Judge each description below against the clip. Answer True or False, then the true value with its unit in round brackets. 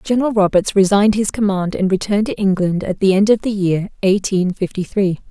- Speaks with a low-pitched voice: False (195 Hz)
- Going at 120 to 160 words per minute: False (205 wpm)